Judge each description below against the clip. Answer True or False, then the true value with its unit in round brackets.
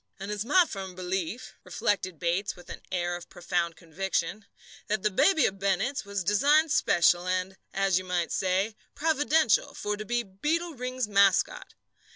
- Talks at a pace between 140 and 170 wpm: True (165 wpm)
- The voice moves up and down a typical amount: True (4.6 semitones)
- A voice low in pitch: False (195 Hz)